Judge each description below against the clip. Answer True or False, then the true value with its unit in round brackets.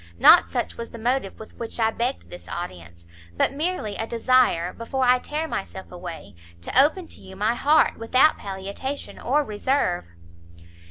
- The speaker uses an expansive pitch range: True (5.9 semitones)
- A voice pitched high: True (230 Hz)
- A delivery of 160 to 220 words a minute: True (165 wpm)